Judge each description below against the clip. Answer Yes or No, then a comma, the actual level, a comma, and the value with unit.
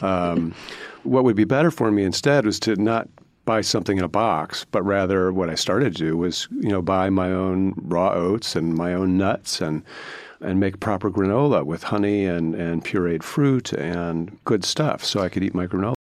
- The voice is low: Yes, very low, 95 Hz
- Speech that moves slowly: No, fast, 205 wpm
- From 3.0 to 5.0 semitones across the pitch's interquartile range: Yes, average, 3.4 semitones